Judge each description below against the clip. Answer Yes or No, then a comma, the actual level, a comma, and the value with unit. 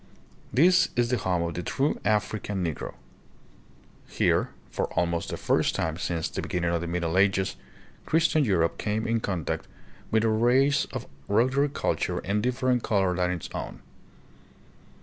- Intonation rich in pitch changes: Yes, wide, 5.8 semitones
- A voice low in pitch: Yes, low, 100 Hz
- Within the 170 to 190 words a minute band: No, average, 160 wpm